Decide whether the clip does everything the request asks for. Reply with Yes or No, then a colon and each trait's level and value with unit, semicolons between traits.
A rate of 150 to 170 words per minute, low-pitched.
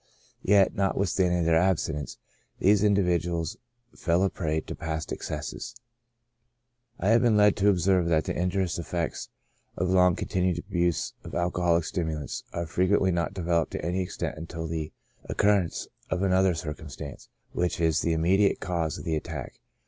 Yes: average, 160 wpm; very low, 90 Hz